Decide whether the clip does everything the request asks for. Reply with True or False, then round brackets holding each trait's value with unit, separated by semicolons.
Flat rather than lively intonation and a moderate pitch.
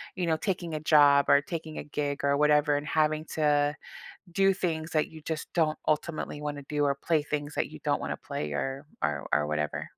True (1.8 semitones; 150 Hz)